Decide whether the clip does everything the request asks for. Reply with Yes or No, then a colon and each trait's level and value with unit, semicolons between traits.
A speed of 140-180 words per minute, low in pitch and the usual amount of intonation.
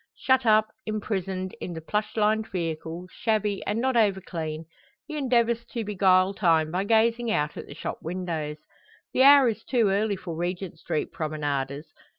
No: average, 165 wpm; high, 195 Hz; average, 5.0 semitones